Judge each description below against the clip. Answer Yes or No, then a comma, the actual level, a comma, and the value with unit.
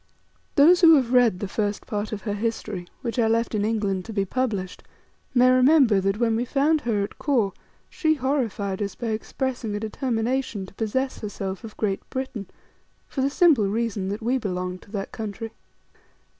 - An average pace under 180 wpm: No, average, 185 wpm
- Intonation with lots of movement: No, average, 4.1 semitones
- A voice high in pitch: Yes, high, 225 Hz